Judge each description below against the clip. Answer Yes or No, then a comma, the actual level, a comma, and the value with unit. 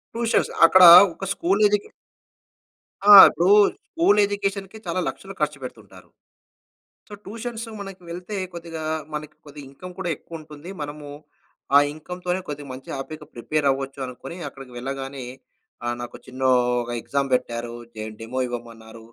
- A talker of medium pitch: Yes, medium, 150 Hz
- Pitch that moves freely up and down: Yes, wide, 6.1 semitones